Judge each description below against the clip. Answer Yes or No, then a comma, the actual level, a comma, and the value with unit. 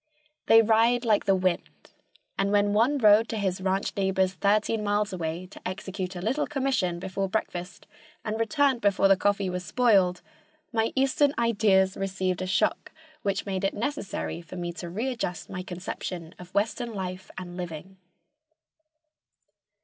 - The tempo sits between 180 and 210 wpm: No, average, 155 wpm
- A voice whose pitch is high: Yes, high, 195 Hz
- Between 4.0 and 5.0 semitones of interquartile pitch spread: No, average, 3.3 semitones